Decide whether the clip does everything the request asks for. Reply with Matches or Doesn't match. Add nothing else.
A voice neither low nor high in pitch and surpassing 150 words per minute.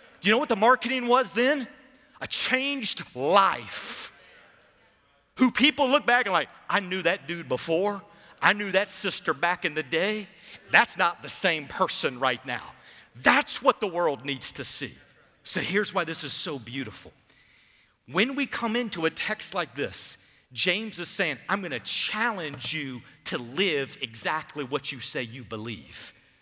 Matches